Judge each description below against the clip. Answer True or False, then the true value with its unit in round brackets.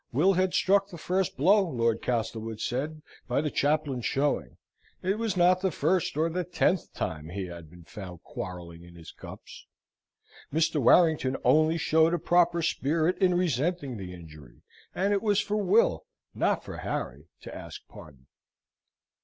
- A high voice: False (155 Hz)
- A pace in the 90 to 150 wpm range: False (160 wpm)